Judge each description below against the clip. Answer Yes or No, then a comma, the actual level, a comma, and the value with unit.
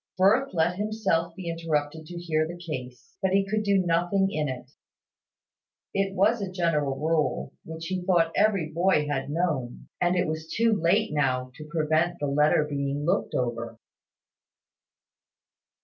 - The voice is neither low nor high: Yes, medium, 165 Hz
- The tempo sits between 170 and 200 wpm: No, average, 155 wpm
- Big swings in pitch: No, average, 4.0 semitones